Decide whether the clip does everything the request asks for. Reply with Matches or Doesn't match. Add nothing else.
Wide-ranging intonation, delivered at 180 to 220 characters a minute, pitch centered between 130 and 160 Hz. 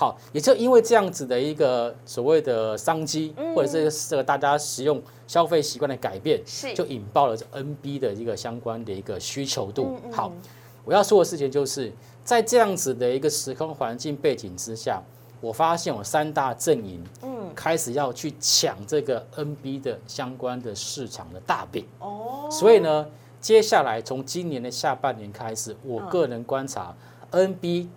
Doesn't match